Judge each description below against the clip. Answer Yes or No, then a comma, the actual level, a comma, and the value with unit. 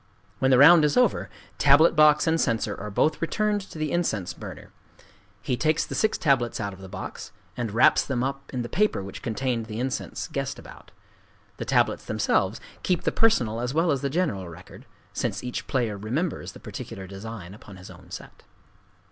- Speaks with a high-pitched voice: No, low, 125 Hz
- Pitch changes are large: Yes, wide, 6.5 semitones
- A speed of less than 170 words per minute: No, average, 190 wpm